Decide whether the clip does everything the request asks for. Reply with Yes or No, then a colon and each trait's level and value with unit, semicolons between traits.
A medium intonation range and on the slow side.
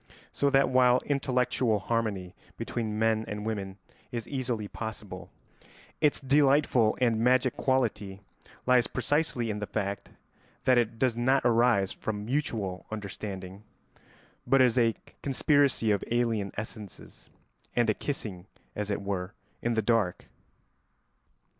Yes: average, 3.5 semitones; slow, 130 wpm